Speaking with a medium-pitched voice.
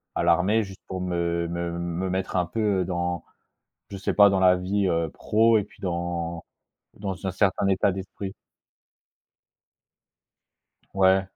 No: very low, 95 Hz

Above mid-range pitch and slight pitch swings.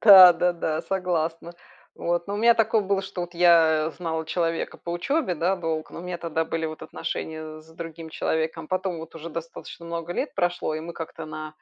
No: medium, 170 Hz; narrow, 1.9 semitones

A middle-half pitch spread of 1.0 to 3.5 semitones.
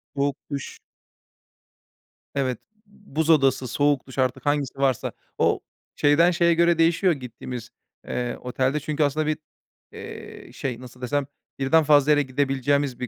Yes: average, 2.9 semitones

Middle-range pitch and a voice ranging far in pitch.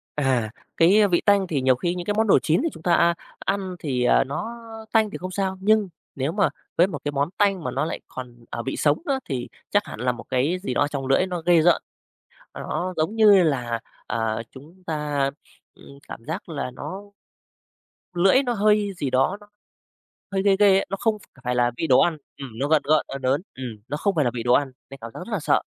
Yes: medium, 160 Hz; wide, 6.6 semitones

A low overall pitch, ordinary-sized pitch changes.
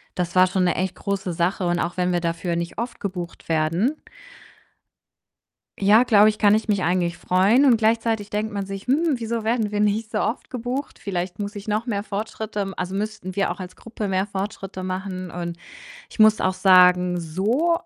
No: high, 195 Hz; average, 3.1 semitones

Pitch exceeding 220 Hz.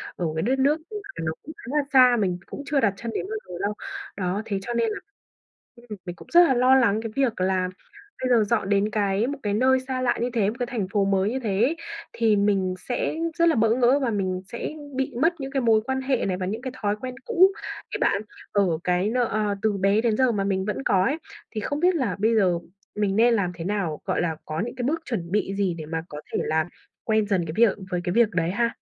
No: high, 215 Hz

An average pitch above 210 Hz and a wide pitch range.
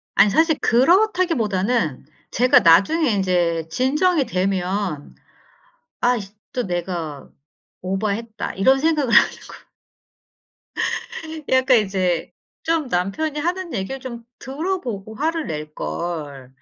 Yes: high, 220 Hz; wide, 7.8 semitones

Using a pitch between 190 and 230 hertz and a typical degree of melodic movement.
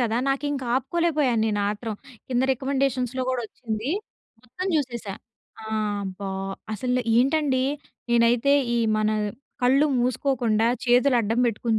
No: high, 245 Hz; average, 3.0 semitones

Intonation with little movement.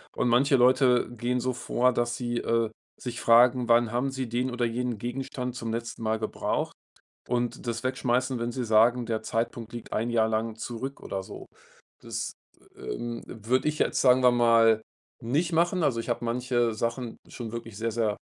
Yes: narrow, 1.5 semitones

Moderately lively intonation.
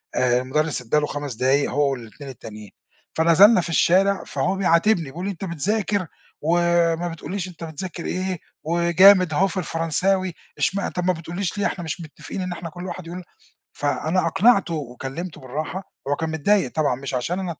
Yes: average, 4.0 semitones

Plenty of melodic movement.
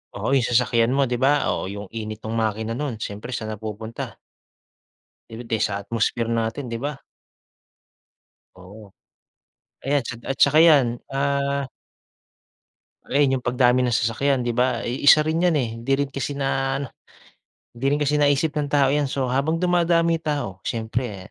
No: average, 3.8 semitones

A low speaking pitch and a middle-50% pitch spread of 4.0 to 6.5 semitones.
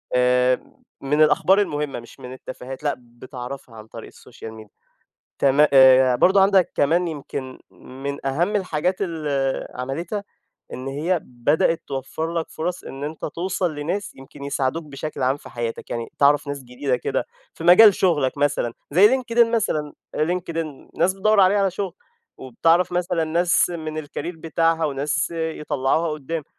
No: medium, 150 Hz; average, 4.6 semitones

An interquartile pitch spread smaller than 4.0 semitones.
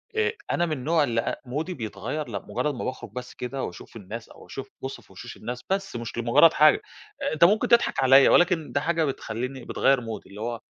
No: average, 5.2 semitones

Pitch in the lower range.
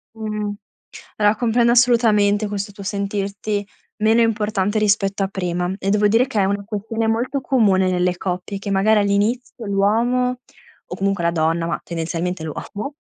No: high, 205 Hz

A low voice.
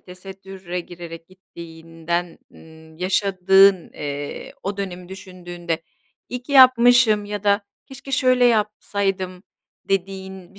No: high, 190 Hz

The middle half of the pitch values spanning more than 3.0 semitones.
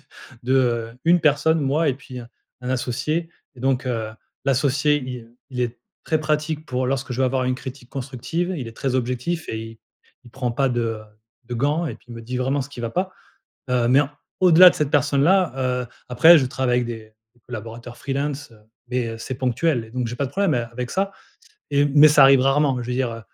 Yes: average, 3.4 semitones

